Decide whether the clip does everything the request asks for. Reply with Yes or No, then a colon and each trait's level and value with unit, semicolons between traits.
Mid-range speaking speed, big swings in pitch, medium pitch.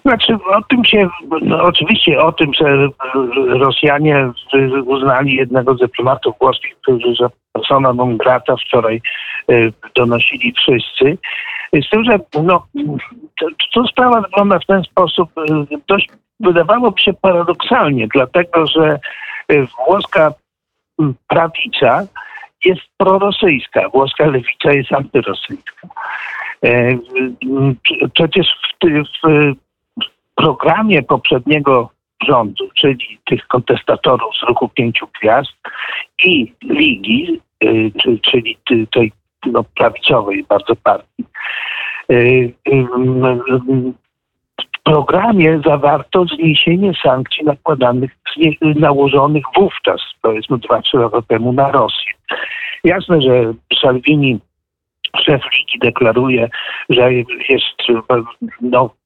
No: slow, 100 wpm; wide, 7.1 semitones; medium, 150 Hz